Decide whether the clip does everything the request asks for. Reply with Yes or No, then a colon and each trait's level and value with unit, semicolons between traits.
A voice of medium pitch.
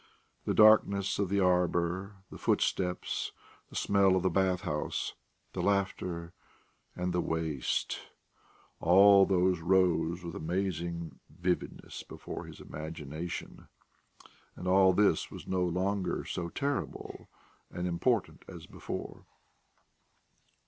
No: very low, 90 Hz